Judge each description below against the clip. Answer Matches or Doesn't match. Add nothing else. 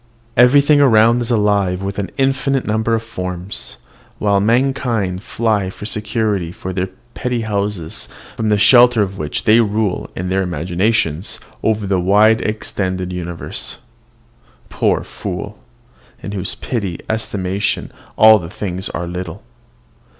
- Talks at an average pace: Doesn't match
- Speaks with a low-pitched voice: Matches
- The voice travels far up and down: Doesn't match